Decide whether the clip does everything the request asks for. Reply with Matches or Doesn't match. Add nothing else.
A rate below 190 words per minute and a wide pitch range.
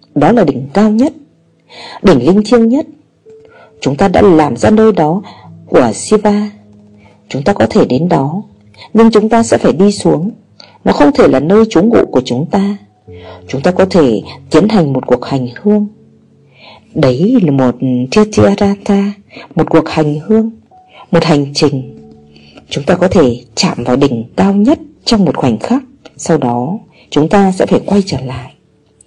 Matches